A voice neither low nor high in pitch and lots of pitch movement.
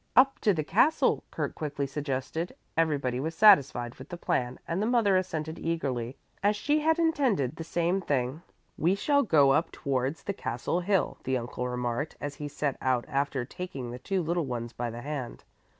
Yes: medium, 150 Hz; wide, 6.3 semitones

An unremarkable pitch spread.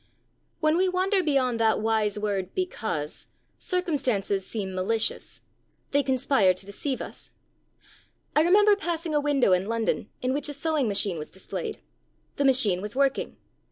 No: wide, 7.0 semitones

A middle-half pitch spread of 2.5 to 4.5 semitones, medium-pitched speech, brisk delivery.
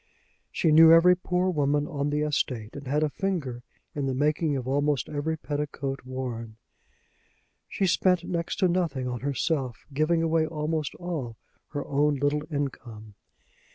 No: average, 3.3 semitones; medium, 145 Hz; average, 155 wpm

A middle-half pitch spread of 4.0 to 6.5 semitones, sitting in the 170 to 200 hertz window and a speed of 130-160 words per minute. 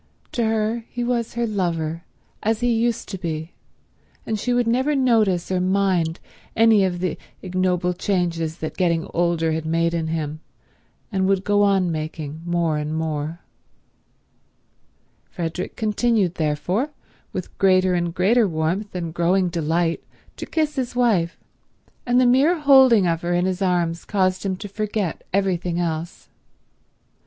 Yes: average, 4.5 semitones; medium, 185 Hz; average, 150 wpm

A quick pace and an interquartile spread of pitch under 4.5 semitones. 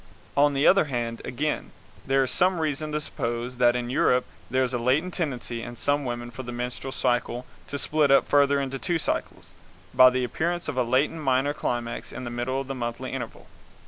Yes: fast, 210 wpm; average, 3.0 semitones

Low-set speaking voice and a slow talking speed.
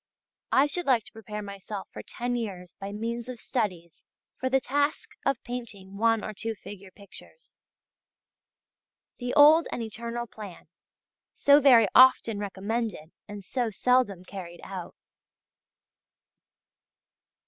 No: high, 225 Hz; slow, 125 wpm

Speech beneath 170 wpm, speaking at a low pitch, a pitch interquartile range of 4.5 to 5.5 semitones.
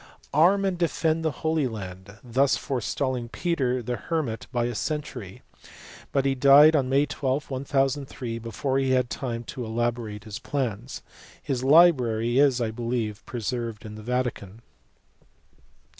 No: average, 150 wpm; low, 125 Hz; average, 3.2 semitones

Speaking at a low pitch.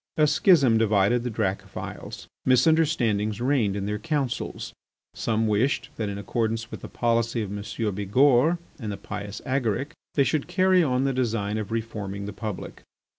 Yes: low, 115 Hz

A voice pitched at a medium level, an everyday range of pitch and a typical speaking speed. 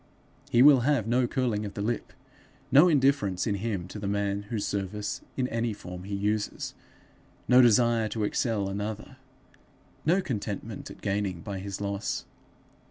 No: low, 105 Hz; average, 3.2 semitones; average, 160 wpm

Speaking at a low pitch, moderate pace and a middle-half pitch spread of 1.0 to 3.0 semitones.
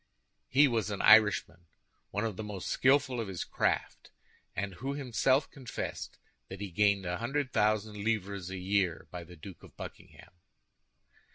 No: low, 105 Hz; average, 155 wpm; average, 3.8 semitones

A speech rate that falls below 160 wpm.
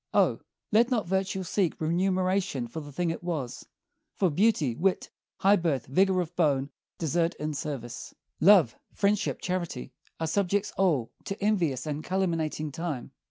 Yes: average, 150 wpm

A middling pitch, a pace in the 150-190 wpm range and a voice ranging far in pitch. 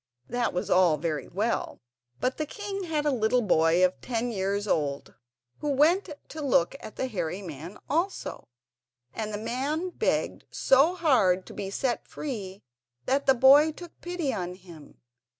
No: high, 235 Hz; average, 165 wpm; wide, 8.1 semitones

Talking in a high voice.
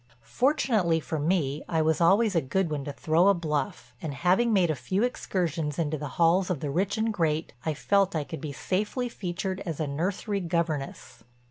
No: medium, 170 Hz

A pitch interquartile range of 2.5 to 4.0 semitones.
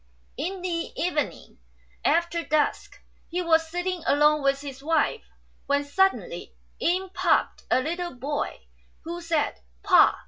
Yes: average, 3.5 semitones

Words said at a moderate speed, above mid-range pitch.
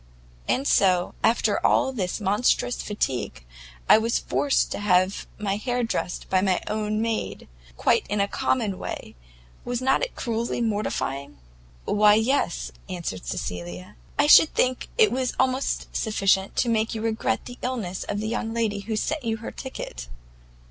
Yes: average, 160 wpm; high, 215 Hz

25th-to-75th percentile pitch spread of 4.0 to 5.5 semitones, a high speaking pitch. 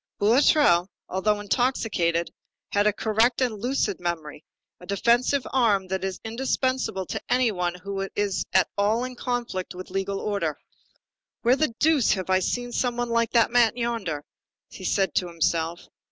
Yes: average, 4.5 semitones; high, 205 Hz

